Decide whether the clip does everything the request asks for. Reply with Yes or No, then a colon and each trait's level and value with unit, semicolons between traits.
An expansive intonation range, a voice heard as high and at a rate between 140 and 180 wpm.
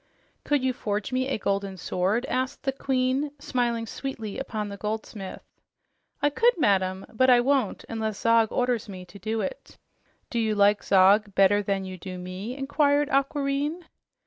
No: average, 5.0 semitones; high, 225 Hz; average, 165 wpm